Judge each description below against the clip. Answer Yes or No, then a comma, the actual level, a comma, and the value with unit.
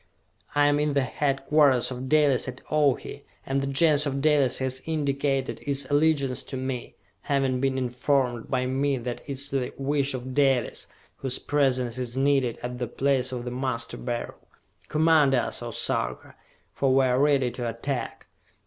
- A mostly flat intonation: Yes, narrow, 2.0 semitones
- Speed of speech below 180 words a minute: Yes, average, 170 wpm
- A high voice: No, low, 135 Hz